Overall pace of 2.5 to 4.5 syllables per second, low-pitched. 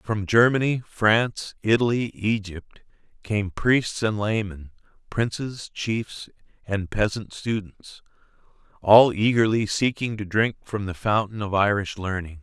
Yes: 4.0 syllables/s; low, 105 Hz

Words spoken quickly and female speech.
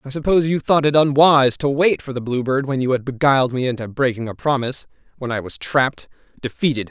No: fast, 215 wpm; male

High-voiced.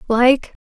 Yes: high, 245 Hz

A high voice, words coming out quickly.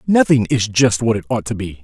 No: low, 115 Hz; fast, 260 wpm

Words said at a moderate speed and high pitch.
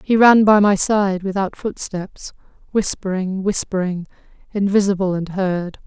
No: slow, 110 wpm; high, 195 Hz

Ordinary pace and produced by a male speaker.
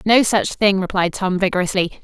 No: average, 175 wpm; female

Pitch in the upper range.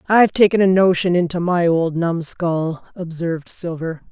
No: medium, 175 Hz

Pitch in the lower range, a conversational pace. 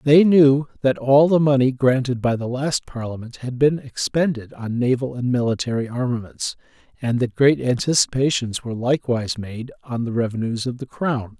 Yes: low, 125 Hz; average, 170 wpm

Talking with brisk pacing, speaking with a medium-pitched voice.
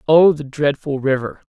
No: average, 160 wpm; medium, 145 Hz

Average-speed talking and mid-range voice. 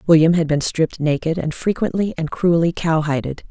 Yes: average, 170 wpm; medium, 165 Hz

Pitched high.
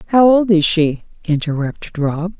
No: medium, 175 Hz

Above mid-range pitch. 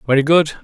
No: medium, 145 Hz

